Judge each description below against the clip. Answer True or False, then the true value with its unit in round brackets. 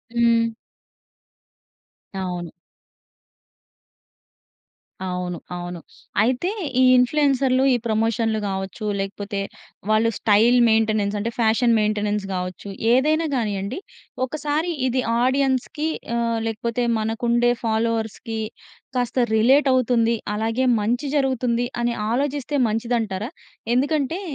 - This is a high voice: True (230 Hz)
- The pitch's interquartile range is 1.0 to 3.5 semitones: True (3.2 semitones)